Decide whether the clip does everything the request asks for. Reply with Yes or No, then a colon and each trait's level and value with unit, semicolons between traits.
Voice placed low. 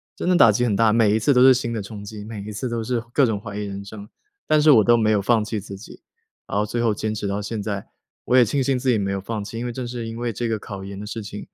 Yes: low, 110 Hz